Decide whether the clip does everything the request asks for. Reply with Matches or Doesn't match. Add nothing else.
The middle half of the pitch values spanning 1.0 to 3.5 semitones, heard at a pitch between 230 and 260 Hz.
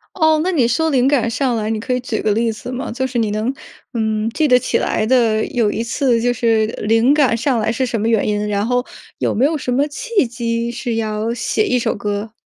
Matches